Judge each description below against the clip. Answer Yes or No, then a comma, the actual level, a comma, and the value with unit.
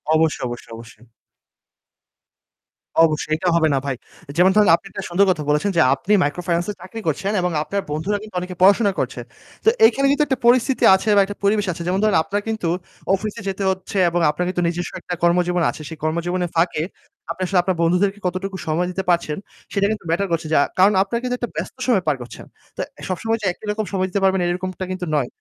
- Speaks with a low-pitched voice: No, medium, 185 Hz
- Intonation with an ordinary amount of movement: Yes, average, 3.2 semitones